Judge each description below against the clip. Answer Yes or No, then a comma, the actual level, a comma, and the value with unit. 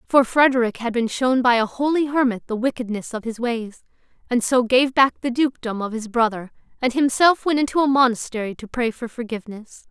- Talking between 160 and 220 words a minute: Yes, average, 200 wpm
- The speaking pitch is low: No, high, 245 Hz